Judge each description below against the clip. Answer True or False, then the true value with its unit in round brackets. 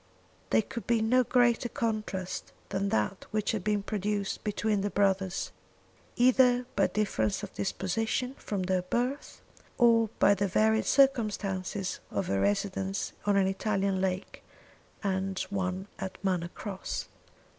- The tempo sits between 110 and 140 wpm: True (135 wpm)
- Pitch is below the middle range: False (200 Hz)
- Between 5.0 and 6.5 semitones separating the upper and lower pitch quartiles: False (2.7 semitones)